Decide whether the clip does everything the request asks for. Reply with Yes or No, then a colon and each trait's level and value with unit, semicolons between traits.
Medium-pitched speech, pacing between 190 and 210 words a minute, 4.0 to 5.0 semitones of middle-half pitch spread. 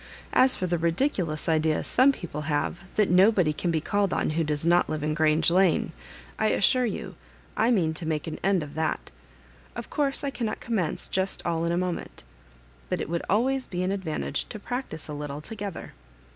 Yes: medium, 175 Hz; average, 200 wpm; average, 4.6 semitones